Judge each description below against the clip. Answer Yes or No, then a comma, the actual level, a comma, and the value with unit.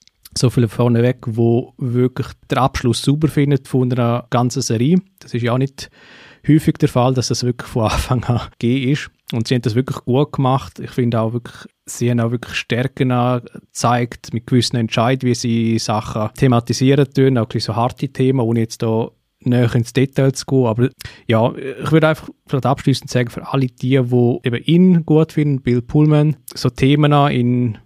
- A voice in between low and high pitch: No, low, 125 Hz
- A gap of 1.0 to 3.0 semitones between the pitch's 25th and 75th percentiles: Yes, narrow, 2.5 semitones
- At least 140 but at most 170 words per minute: No, fast, 190 wpm